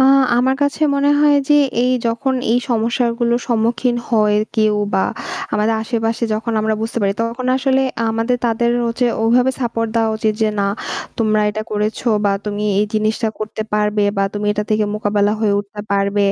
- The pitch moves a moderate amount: No, narrow, 2.1 semitones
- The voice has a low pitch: No, high, 225 Hz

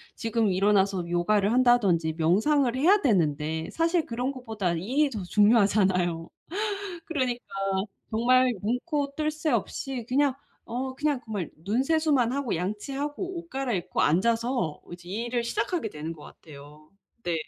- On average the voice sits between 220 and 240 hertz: Yes, high, 230 Hz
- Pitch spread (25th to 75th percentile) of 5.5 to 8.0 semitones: Yes, wide, 6.8 semitones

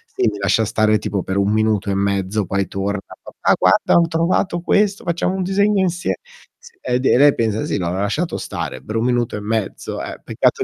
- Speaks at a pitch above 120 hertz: No, low, 110 Hz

